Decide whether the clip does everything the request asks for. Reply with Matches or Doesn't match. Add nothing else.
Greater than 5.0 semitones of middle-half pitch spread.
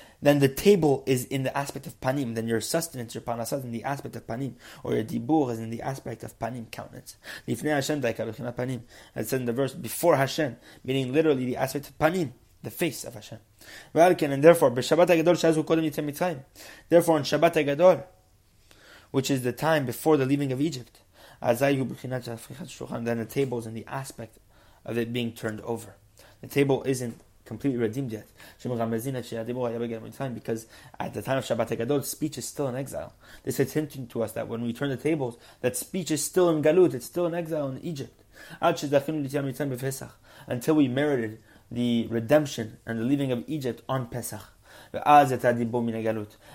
Doesn't match